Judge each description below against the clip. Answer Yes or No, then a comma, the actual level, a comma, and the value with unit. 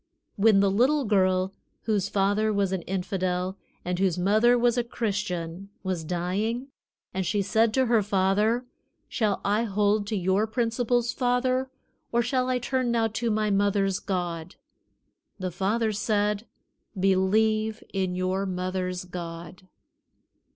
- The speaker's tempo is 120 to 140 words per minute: Yes, slow, 135 wpm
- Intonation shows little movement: No, average, 3.3 semitones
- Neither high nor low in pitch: No, high, 205 Hz